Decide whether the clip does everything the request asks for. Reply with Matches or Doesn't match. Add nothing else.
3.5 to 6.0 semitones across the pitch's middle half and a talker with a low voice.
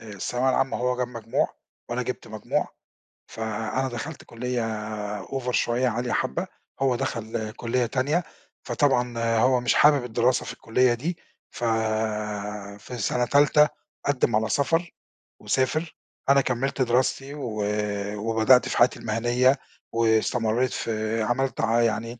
Doesn't match